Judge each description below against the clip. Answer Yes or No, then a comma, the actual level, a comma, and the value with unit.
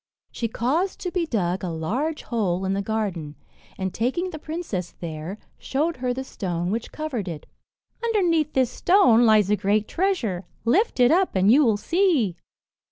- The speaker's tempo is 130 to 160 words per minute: No, average, 170 wpm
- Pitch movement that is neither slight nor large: No, wide, 8.7 semitones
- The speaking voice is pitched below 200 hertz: No, high, 230 Hz